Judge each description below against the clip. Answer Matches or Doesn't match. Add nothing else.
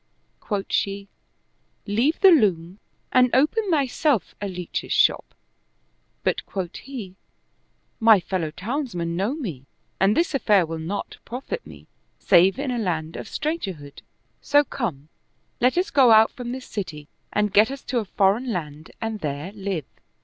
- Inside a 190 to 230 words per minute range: Doesn't match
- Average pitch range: Doesn't match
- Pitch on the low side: Doesn't match